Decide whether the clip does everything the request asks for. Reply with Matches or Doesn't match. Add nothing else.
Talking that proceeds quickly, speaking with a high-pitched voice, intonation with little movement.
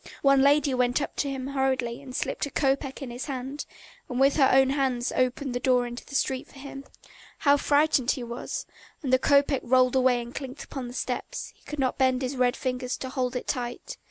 Matches